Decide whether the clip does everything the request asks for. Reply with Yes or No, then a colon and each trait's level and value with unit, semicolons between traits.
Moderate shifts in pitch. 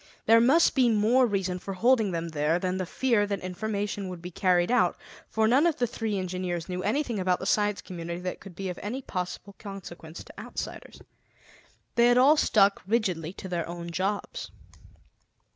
Yes: average, 4.0 semitones